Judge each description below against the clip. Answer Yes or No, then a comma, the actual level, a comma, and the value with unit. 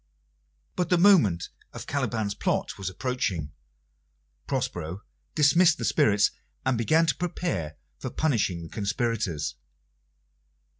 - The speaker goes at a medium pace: No, slow, 110 wpm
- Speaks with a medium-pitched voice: No, low, 115 Hz